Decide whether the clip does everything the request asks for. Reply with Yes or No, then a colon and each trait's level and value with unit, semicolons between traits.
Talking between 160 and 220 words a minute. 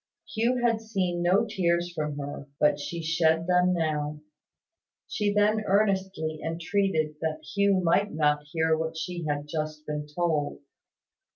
No: average, 145 wpm